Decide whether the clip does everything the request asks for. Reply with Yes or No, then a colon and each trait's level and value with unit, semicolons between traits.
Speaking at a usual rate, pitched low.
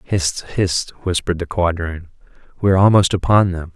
Yes: average, 160 wpm; very low, 90 Hz